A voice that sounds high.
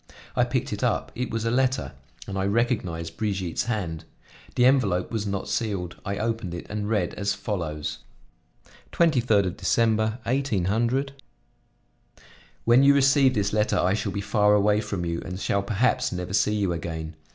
No: low, 105 Hz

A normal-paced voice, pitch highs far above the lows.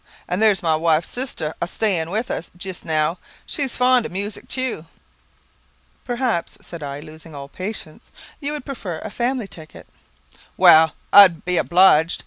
Yes: average, 160 wpm; wide, 5.9 semitones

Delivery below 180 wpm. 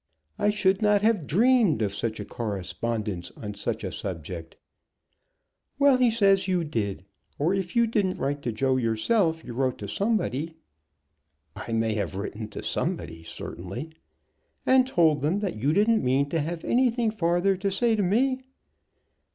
Yes: average, 160 wpm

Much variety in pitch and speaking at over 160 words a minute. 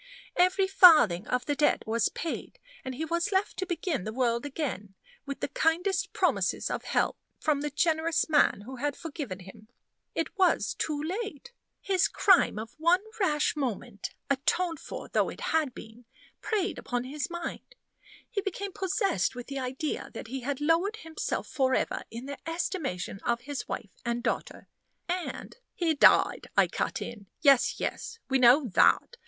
Yes: wide, 6.1 semitones; average, 170 wpm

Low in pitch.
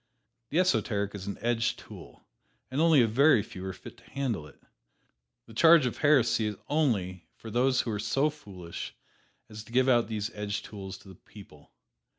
Yes: low, 115 Hz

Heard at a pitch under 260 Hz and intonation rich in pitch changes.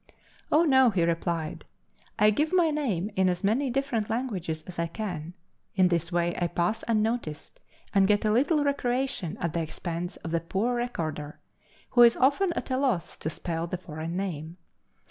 Yes: high, 190 Hz; wide, 6.5 semitones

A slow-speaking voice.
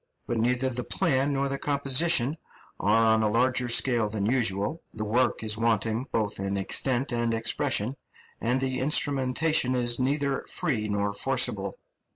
No: average, 155 wpm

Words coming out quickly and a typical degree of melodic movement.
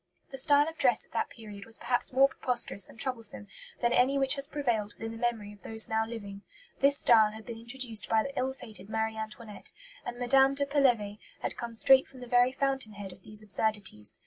Yes: fast, 215 wpm; average, 3.5 semitones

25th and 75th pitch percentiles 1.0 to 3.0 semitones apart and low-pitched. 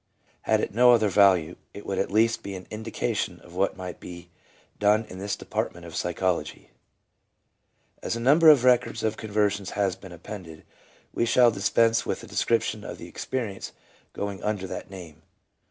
No: average, 3.6 semitones; low, 100 Hz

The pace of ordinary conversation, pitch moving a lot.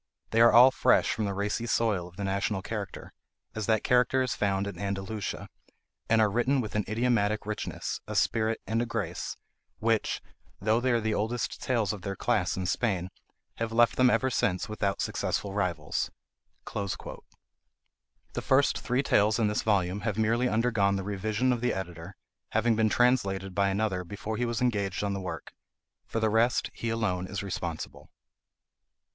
No: average, 175 wpm; average, 2.9 semitones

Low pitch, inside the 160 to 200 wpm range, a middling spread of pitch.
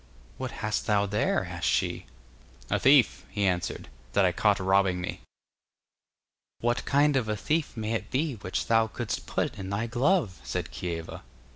Yes: low, 110 Hz; average, 165 wpm; average, 4.9 semitones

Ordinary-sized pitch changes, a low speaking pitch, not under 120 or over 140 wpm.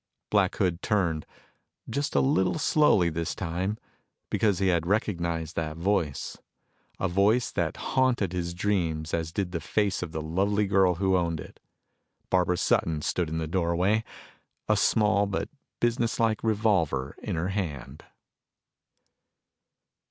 Yes: average, 3.9 semitones; very low, 90 Hz; slow, 135 wpm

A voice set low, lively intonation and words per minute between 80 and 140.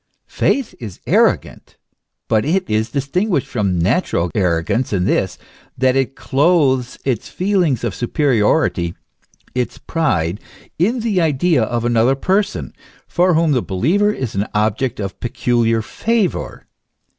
Yes: low, 130 Hz; wide, 7.6 semitones; slow, 135 wpm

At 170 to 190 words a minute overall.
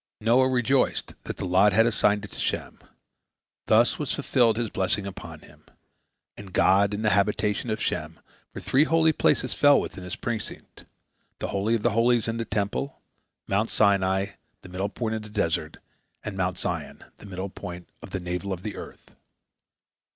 Yes: average, 175 wpm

